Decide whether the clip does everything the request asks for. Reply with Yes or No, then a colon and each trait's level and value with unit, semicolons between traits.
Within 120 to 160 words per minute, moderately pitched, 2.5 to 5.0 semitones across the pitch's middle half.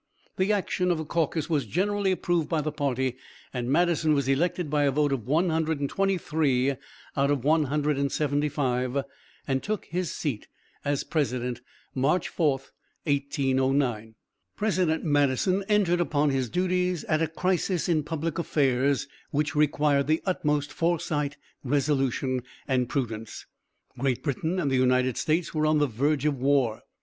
Yes: average, 140 wpm; medium, 145 Hz; average, 3.4 semitones